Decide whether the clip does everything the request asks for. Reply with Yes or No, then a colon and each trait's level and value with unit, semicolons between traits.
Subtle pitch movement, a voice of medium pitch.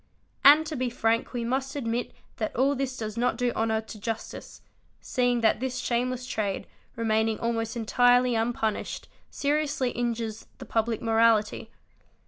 No: narrow, 2.0 semitones; high, 235 Hz